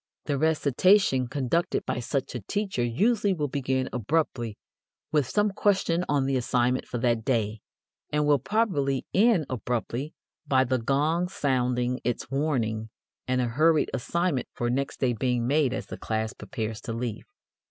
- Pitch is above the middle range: No, low, 130 Hz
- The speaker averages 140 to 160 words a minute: Yes, average, 155 wpm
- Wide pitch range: No, average, 4.4 semitones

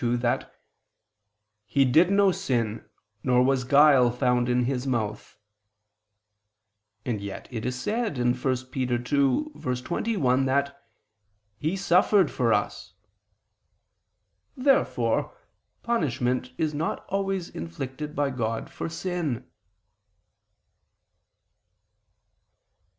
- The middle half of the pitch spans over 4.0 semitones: Yes, average, 4.9 semitones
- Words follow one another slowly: Yes, slow, 95 wpm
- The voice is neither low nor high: No, low, 130 Hz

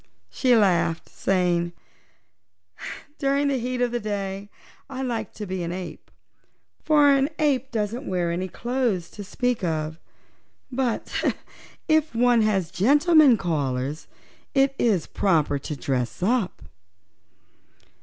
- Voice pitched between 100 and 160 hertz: No, high, 210 Hz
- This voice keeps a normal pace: No, slow, 125 wpm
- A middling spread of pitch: No, wide, 6.6 semitones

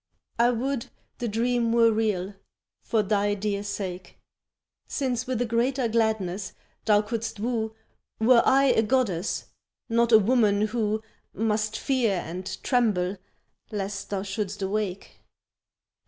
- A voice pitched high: Yes, high, 220 Hz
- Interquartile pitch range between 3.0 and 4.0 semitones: No, narrow, 2.6 semitones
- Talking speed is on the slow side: Yes, slow, 125 wpm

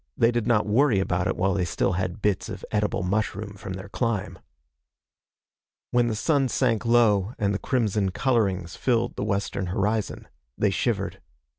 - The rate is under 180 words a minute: Yes, average, 165 wpm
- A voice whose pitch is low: Yes, low, 105 Hz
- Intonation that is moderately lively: Yes, average, 3.4 semitones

